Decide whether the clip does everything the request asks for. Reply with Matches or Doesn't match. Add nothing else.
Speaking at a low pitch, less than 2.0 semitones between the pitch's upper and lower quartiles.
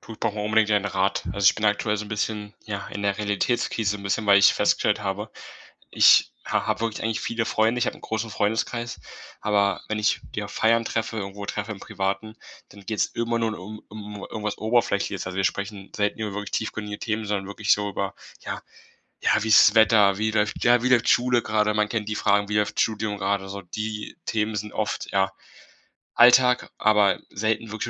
Matches